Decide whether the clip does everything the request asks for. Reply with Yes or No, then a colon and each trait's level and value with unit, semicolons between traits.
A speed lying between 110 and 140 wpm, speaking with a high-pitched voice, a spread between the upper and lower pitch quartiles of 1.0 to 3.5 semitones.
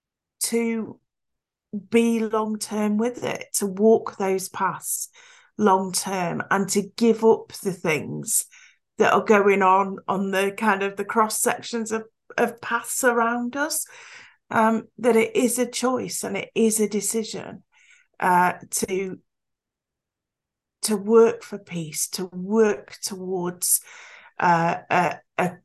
Yes: slow, 135 wpm; high, 215 Hz; average, 3.2 semitones